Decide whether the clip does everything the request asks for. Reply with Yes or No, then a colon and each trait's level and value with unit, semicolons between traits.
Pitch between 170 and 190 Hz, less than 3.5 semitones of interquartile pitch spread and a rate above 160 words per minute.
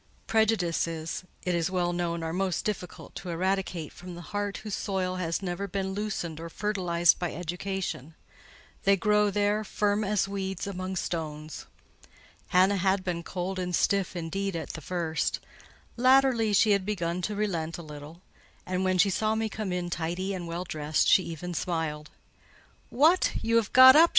Yes: medium, 185 Hz; average, 3.1 semitones; average, 170 wpm